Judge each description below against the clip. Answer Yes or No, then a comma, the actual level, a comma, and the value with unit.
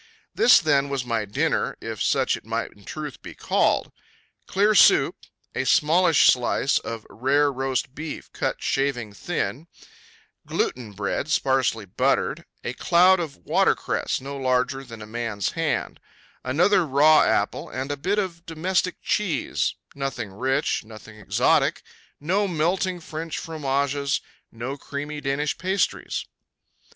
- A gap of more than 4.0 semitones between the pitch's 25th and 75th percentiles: Yes, average, 4.5 semitones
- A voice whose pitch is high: No, medium, 140 Hz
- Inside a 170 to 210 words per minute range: No, slow, 135 wpm